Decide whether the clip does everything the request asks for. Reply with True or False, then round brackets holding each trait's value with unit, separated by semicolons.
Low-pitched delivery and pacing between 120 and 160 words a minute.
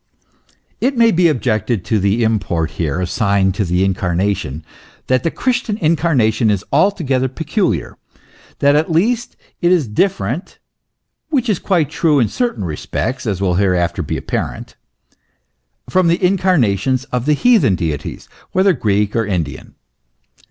True (125 Hz; 145 wpm)